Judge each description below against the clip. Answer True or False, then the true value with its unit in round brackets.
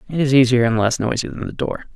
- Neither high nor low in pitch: False (125 Hz)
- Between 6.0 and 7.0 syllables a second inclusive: True (6.3 syllables/s)